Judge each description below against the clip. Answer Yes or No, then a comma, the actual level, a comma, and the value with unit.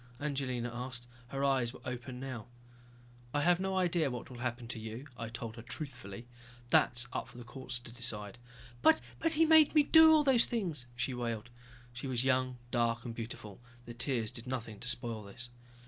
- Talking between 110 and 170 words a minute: No, average, 195 wpm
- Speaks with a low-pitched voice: Yes, low, 125 Hz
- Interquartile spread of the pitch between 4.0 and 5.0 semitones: No, average, 2.8 semitones